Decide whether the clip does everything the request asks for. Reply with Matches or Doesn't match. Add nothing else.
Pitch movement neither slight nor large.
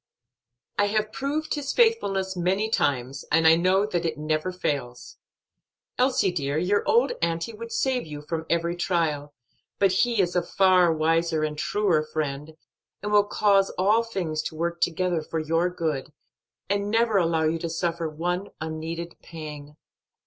Matches